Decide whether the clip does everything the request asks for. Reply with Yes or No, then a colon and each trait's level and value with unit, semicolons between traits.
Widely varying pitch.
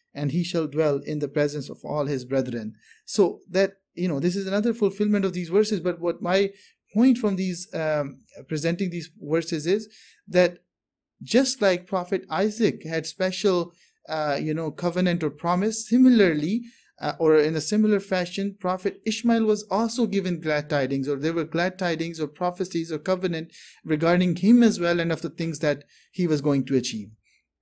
No: average, 4.1 semitones